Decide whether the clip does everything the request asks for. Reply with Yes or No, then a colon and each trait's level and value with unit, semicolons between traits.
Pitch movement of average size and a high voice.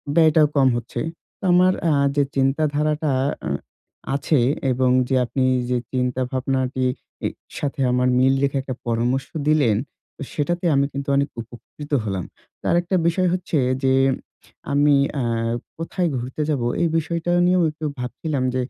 No: average, 3.5 semitones; medium, 140 Hz